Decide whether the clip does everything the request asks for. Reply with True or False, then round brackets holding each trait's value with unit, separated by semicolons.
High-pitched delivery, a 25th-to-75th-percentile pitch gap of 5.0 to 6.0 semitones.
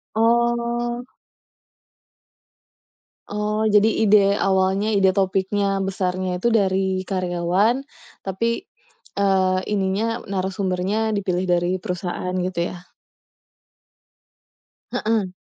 False (195 Hz; 2.5 semitones)